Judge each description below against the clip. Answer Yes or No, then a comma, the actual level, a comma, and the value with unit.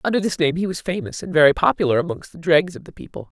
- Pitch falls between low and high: Yes, medium, 170 Hz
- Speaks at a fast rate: Yes, fast, 265 wpm